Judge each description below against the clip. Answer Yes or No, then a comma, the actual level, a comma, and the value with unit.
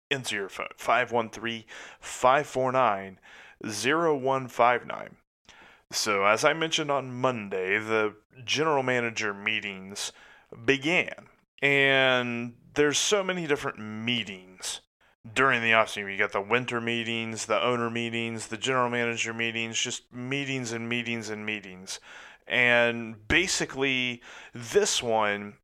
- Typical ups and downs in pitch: Yes, average, 3.2 semitones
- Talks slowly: Yes, slow, 110 wpm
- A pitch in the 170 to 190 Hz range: No, low, 120 Hz